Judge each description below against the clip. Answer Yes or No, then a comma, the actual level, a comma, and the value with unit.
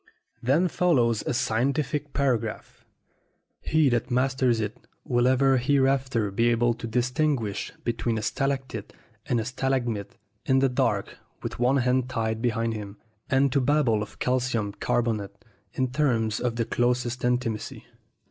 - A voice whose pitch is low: Yes, low, 125 Hz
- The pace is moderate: Yes, average, 145 wpm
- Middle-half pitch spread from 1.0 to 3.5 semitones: Yes, average, 2.7 semitones